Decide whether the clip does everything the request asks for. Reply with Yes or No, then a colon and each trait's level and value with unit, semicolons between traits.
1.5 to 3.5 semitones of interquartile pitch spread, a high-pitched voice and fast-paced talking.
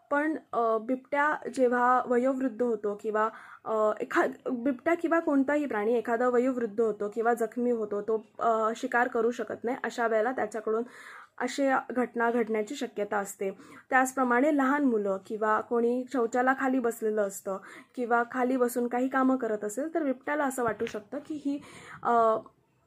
Yes: average, 2.8 semitones; high, 240 Hz; fast, 140 wpm